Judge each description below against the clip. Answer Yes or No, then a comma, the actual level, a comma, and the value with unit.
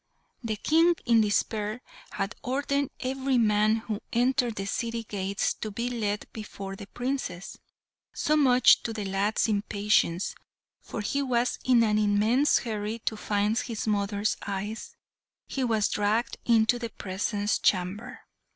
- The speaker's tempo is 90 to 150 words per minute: Yes, average, 140 wpm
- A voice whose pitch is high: Yes, high, 220 Hz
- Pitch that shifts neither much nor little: Yes, average, 3.0 semitones